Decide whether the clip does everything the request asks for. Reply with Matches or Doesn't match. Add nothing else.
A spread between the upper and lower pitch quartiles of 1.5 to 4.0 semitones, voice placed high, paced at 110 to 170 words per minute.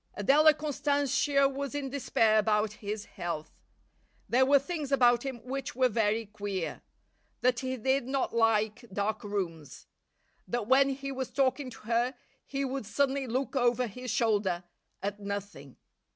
Doesn't match